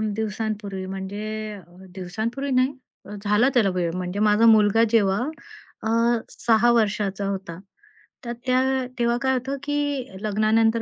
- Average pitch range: Yes, average, 3.0 semitones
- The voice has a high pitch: Yes, high, 215 Hz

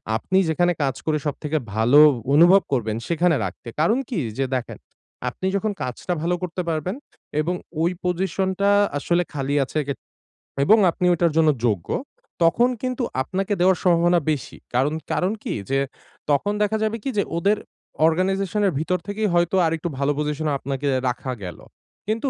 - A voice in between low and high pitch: Yes, medium, 170 Hz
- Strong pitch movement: No, average, 4.7 semitones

